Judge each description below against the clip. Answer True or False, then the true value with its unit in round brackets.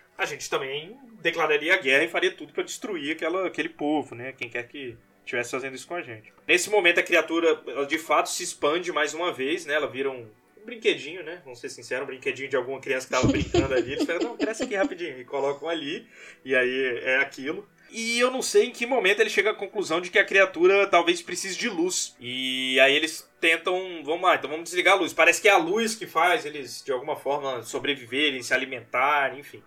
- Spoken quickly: True (225 wpm)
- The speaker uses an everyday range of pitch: False (7.7 semitones)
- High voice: False (175 Hz)